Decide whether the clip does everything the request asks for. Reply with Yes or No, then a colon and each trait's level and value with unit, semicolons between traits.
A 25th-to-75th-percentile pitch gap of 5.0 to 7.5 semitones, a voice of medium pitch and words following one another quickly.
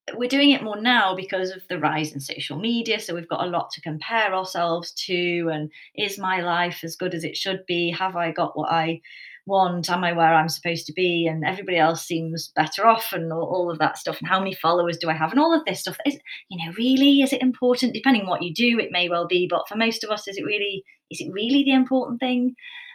Yes: wide, 5.4 semitones; medium, 180 Hz; fast, 255 wpm